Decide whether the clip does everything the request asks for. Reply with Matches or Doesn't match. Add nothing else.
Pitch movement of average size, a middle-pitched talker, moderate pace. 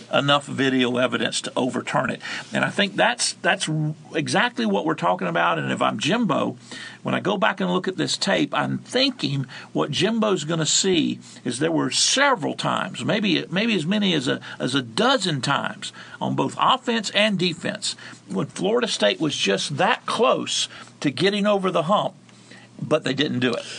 Doesn't match